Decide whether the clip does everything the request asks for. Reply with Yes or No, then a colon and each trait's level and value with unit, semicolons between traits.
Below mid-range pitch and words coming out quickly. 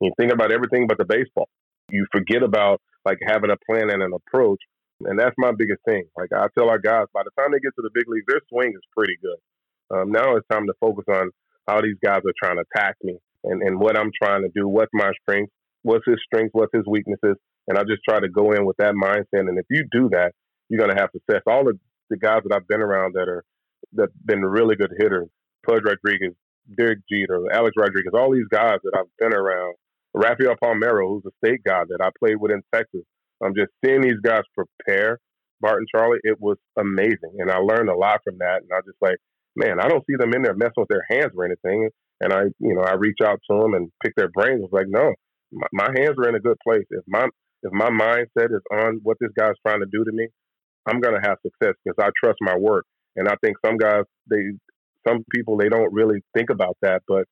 Yes: low, 110 Hz; fast, 245 wpm